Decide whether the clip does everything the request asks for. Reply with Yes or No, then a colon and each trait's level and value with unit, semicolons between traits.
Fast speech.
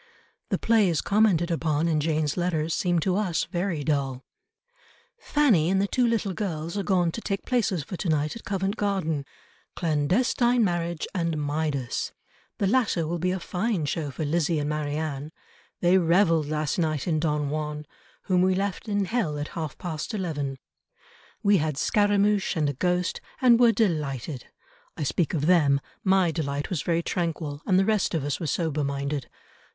No: average, 175 wpm